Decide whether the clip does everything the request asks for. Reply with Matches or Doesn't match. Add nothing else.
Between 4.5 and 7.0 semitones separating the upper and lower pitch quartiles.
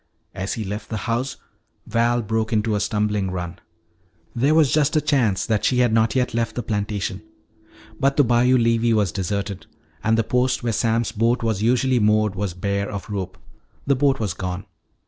Doesn't match